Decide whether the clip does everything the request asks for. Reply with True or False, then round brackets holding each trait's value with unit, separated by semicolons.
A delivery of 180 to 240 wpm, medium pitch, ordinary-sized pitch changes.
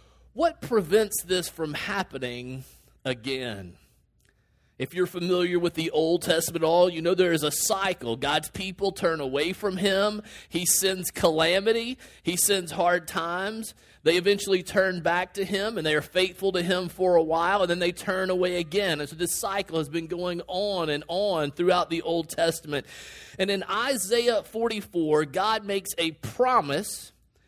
False (170 wpm; 180 Hz; 3.1 semitones)